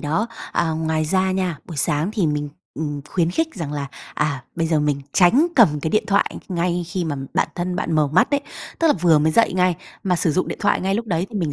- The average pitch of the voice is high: No, medium, 170 Hz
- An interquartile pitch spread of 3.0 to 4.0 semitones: Yes, average, 3.6 semitones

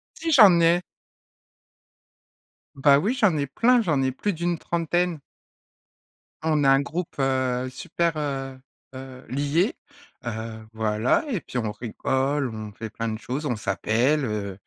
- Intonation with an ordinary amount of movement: No, wide, 6.0 semitones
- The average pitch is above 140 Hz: No, low, 135 Hz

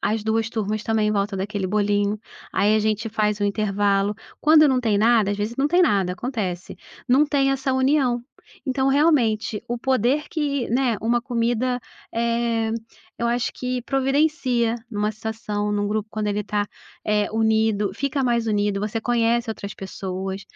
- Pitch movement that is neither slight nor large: Yes, average, 3.3 semitones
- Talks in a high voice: Yes, high, 225 Hz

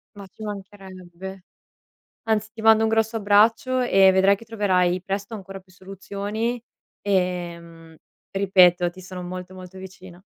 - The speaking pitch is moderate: No, high, 195 Hz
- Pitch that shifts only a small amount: Yes, narrow, 2.3 semitones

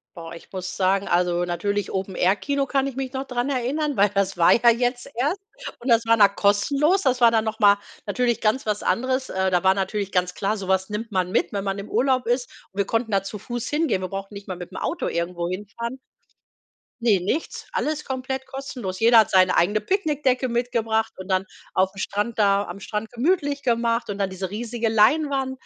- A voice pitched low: No, high, 220 Hz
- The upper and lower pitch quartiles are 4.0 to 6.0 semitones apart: Yes, average, 4.7 semitones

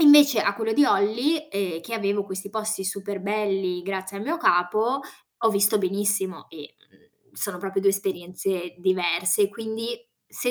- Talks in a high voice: Yes, high, 200 Hz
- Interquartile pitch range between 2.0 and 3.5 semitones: Yes, average, 2.7 semitones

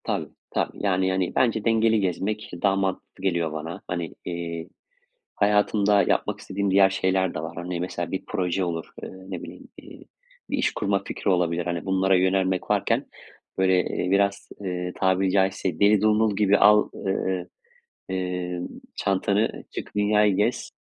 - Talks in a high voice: No, very low, 95 Hz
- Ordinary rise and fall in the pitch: No, narrow, 2.1 semitones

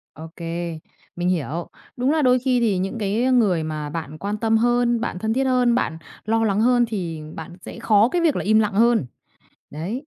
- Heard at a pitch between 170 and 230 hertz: Yes, high, 215 Hz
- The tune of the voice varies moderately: No, wide, 5.8 semitones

